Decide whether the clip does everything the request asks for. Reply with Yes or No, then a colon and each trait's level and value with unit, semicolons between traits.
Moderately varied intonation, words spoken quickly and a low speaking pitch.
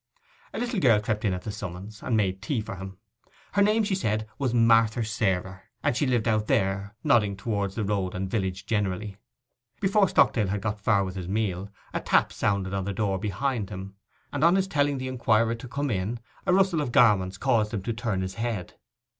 Yes: average, 3.8 semitones; fast, 210 wpm; low, 105 Hz